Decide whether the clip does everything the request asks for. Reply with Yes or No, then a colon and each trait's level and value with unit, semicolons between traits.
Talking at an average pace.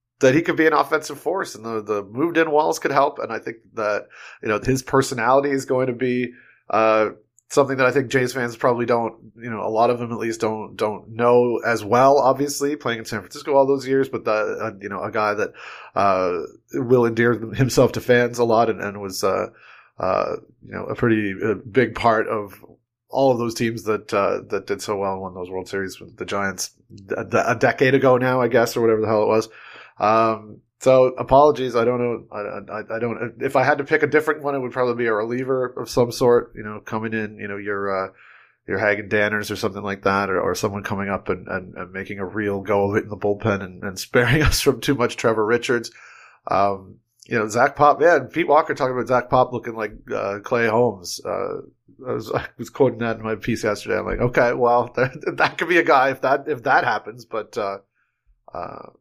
No: fast, 235 wpm